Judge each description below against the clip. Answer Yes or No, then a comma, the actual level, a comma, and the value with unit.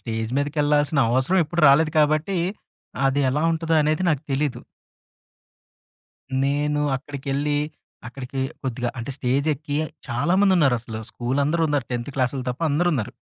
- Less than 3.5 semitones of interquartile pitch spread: Yes, average, 2.9 semitones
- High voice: No, medium, 145 Hz